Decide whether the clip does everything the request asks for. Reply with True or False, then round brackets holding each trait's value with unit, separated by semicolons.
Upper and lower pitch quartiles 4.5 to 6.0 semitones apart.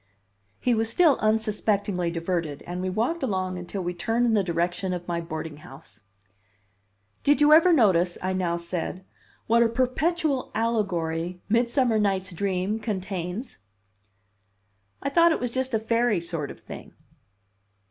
True (5.0 semitones)